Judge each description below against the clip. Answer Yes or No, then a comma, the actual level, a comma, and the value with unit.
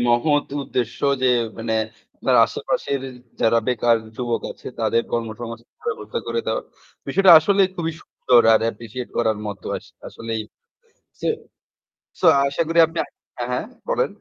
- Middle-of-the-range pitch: No, low, 120 Hz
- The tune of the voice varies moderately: No, wide, 5.9 semitones